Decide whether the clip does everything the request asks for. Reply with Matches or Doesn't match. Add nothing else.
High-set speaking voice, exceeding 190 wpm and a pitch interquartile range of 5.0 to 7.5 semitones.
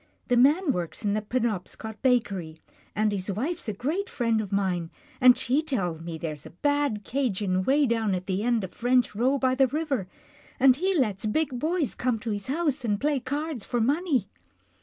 Matches